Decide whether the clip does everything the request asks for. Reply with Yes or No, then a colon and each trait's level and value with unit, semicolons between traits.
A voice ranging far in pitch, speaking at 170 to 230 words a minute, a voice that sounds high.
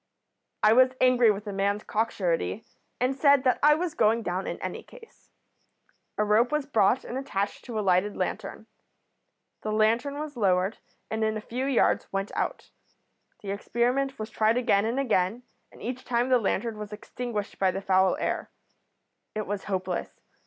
No: average, 3.9 semitones; average, 175 wpm; high, 220 Hz